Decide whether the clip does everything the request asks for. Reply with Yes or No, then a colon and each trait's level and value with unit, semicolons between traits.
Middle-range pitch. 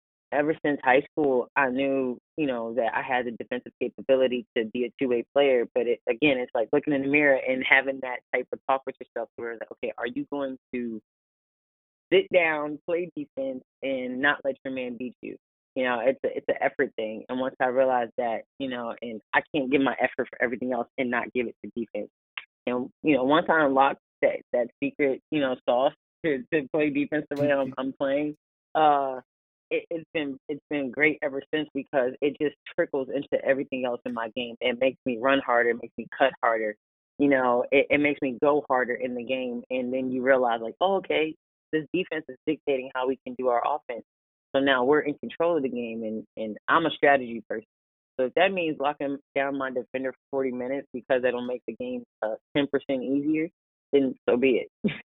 No: low, 130 Hz